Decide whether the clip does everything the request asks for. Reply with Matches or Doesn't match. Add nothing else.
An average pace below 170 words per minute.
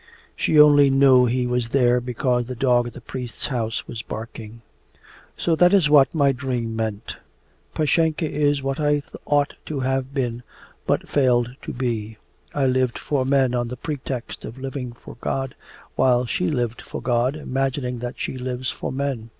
Doesn't match